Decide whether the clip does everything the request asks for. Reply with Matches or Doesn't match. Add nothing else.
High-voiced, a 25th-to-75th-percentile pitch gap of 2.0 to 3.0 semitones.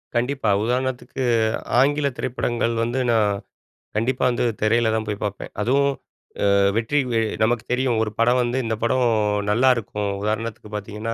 Doesn't match